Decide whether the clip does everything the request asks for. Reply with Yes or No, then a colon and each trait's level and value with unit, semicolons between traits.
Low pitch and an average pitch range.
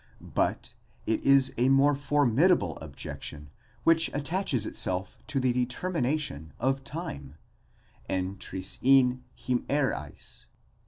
No: low, 130 Hz; wide, 7.2 semitones